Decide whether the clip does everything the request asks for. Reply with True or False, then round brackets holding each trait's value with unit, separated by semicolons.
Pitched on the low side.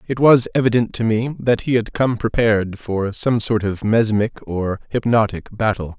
True (110 Hz)